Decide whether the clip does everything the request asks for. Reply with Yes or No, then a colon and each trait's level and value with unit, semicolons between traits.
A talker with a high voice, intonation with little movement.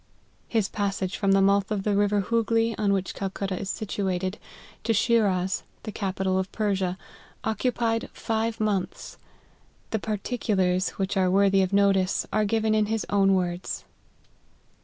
Yes: high, 200 Hz; narrow, 2.2 semitones